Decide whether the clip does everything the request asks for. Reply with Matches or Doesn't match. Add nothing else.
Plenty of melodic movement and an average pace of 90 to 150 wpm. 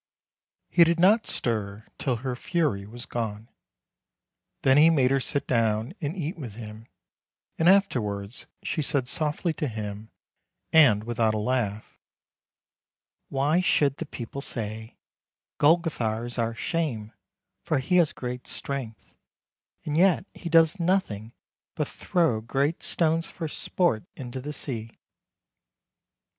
Matches